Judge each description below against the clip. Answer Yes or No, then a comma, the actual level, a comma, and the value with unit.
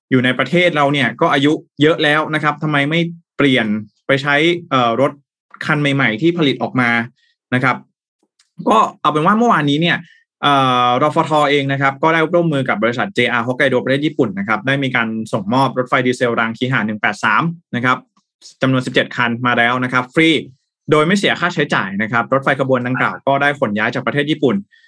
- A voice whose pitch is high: No, low, 135 Hz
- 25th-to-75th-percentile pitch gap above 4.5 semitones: No, average, 3.7 semitones